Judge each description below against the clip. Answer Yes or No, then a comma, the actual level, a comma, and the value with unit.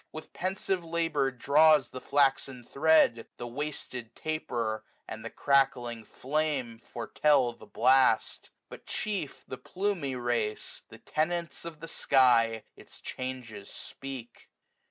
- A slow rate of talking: Yes, slow, 125 wpm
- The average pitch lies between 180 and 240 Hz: No, low, 135 Hz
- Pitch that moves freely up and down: No, average, 4.5 semitones